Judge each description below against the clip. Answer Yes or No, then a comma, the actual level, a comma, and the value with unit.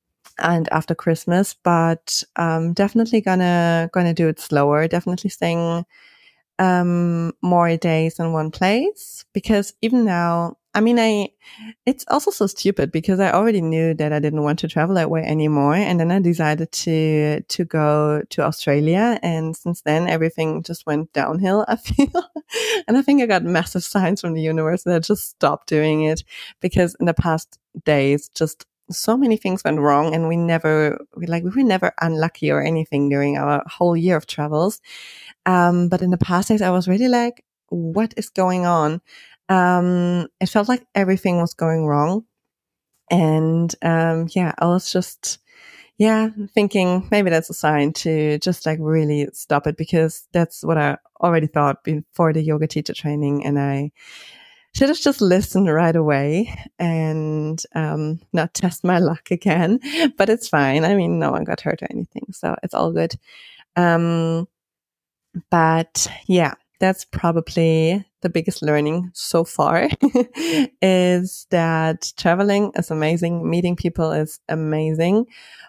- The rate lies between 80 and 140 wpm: No, average, 160 wpm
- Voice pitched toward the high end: No, medium, 170 Hz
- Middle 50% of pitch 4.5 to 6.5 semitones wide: No, average, 3.3 semitones